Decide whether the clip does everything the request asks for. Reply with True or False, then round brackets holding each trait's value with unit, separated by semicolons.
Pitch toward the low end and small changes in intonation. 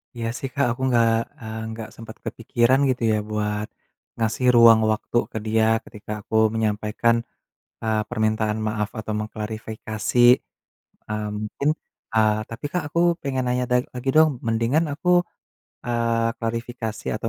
True (115 Hz; 2.0 semitones)